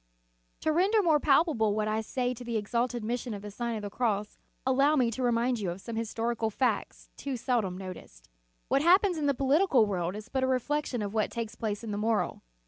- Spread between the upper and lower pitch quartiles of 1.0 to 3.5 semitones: No, average, 3.9 semitones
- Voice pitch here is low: No, high, 235 Hz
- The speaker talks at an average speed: No, fast, 220 wpm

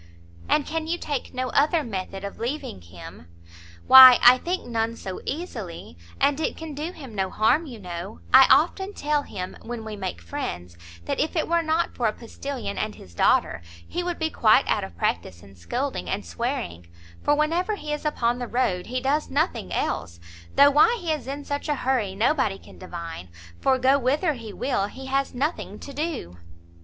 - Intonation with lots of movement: Yes, wide, 7.1 semitones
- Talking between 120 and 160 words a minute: No, average, 195 wpm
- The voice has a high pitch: Yes, very high, 255 Hz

